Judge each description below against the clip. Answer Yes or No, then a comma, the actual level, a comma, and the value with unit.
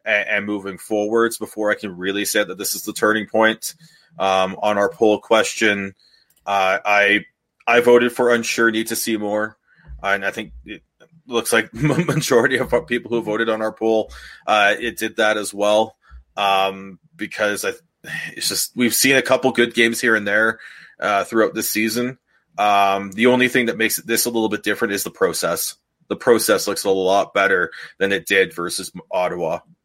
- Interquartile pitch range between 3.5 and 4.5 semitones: No, average, 2.7 semitones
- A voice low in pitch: Yes, low, 110 Hz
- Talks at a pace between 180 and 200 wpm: Yes, average, 185 wpm